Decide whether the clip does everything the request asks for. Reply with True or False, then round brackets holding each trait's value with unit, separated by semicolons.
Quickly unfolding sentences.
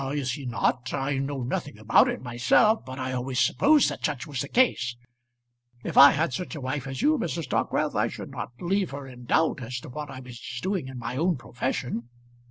True (215 wpm)